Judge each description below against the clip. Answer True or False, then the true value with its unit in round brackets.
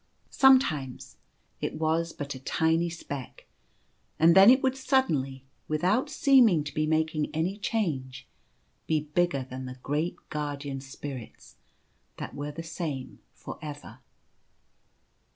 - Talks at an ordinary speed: False (125 wpm)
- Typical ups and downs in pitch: True (3.8 semitones)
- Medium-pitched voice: True (155 Hz)